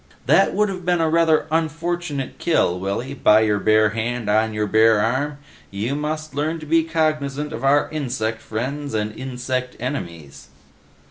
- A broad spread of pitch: Yes, wide, 6.1 semitones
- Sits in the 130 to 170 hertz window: Yes, low, 135 Hz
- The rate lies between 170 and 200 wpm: No, average, 160 wpm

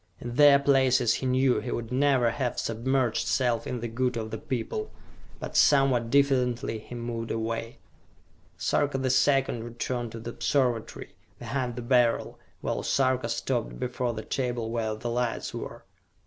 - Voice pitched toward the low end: Yes, low, 120 Hz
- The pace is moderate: Yes, average, 160 wpm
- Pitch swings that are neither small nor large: No, narrow, 2.2 semitones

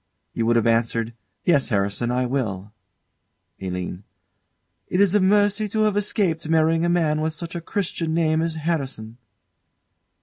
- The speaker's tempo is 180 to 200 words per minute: No, average, 155 wpm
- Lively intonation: Yes, wide, 6.8 semitones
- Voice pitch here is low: No, medium, 160 Hz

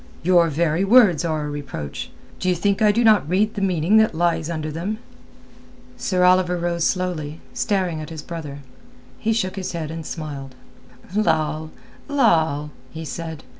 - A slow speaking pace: No, average, 160 wpm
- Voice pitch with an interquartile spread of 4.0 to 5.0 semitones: No, average, 3.4 semitones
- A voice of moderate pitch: Yes, medium, 170 Hz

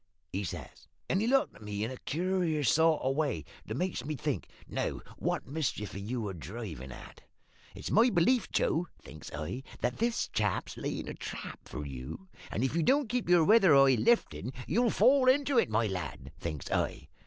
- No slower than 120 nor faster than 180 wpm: No, average, 200 wpm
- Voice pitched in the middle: Yes, medium, 145 Hz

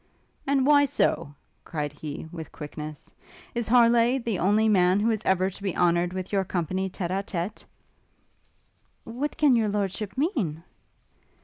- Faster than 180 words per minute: No, average, 150 wpm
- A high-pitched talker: Yes, high, 195 Hz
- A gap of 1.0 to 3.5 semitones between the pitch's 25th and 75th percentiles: No, average, 4.9 semitones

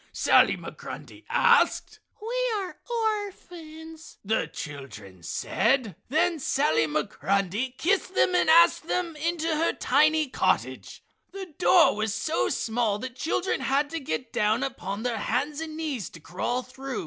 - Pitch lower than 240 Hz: No, very high, 290 Hz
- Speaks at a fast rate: No, average, 140 wpm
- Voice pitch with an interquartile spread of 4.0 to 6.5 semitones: No, wide, 7.3 semitones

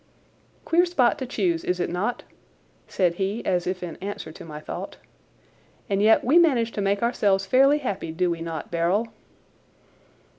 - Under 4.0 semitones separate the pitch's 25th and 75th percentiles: No, average, 5.3 semitones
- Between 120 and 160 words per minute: No, average, 170 wpm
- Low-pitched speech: No, high, 195 Hz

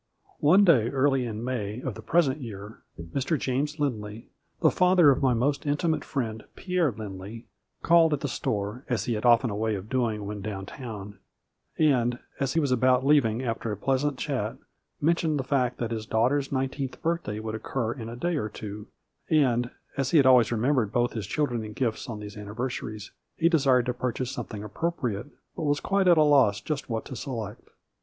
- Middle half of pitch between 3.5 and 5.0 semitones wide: Yes, average, 4.7 semitones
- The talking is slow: No, average, 195 wpm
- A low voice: Yes, low, 125 Hz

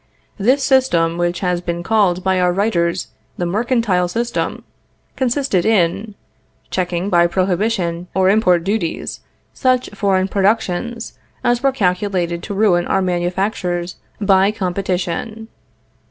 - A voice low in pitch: No, high, 190 Hz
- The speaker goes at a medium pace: No, slow, 120 wpm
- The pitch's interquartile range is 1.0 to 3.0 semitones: No, average, 3.8 semitones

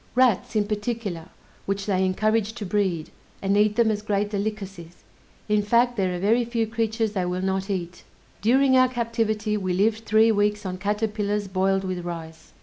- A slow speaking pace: No, average, 175 wpm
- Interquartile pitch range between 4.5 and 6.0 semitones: No, narrow, 2.6 semitones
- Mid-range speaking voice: No, high, 205 Hz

